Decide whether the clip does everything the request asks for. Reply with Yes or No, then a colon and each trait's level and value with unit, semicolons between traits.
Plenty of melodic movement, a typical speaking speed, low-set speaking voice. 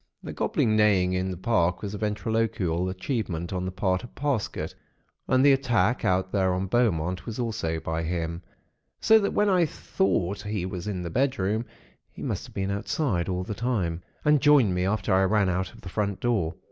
No: average, 4.0 semitones; average, 195 wpm; very low, 95 Hz